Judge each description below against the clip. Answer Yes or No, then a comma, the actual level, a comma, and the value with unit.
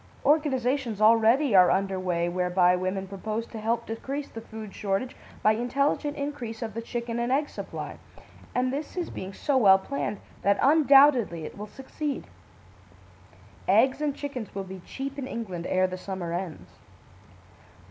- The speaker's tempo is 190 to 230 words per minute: No, average, 155 wpm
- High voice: Yes, high, 225 Hz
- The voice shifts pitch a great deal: Yes, wide, 5.9 semitones